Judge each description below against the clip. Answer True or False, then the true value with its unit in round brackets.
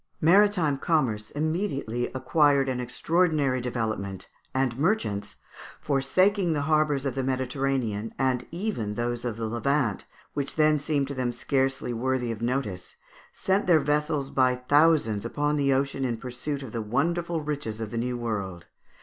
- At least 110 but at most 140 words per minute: False (150 wpm)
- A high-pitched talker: False (135 Hz)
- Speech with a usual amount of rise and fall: True (4.0 semitones)